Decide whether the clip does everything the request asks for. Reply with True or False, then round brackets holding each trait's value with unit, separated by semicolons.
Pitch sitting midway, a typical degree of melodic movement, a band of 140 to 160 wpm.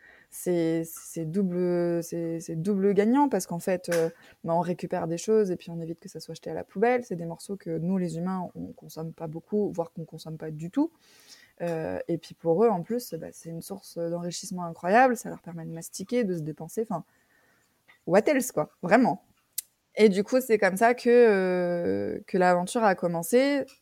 False (175 Hz; 3.7 semitones; 210 wpm)